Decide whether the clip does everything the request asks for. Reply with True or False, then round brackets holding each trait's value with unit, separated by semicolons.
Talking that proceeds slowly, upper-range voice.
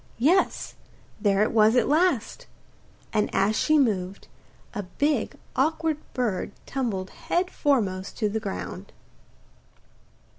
True (115 wpm; 225 Hz)